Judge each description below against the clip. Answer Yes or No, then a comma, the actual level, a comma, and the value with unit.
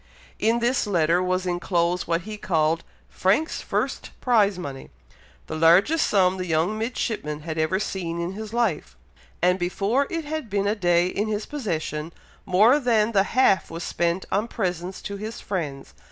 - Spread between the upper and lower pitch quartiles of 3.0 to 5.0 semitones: Yes, average, 4.2 semitones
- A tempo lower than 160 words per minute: No, average, 170 wpm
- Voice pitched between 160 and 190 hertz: Yes, medium, 185 Hz